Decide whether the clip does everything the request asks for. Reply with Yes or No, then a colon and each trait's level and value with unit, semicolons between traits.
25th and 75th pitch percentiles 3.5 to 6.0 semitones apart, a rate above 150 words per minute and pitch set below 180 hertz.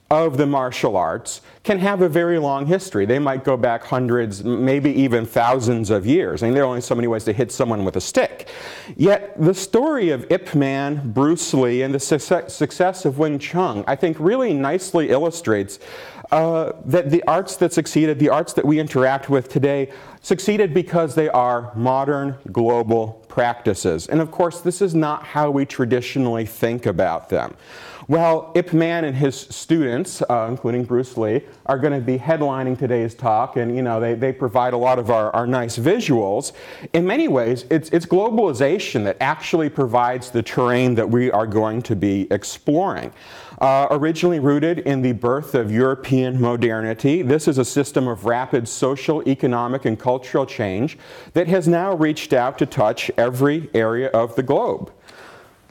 Yes: average, 4.7 semitones; average, 180 wpm; low, 135 Hz